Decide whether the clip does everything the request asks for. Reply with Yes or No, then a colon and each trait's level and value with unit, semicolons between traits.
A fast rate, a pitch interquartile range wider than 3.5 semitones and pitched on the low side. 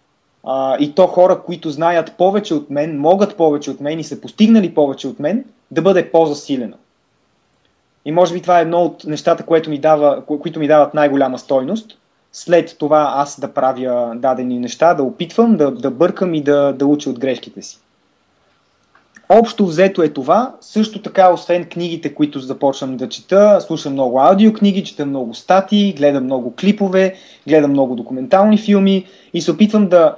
No: fast, 175 wpm; average, 5.2 semitones; medium, 160 Hz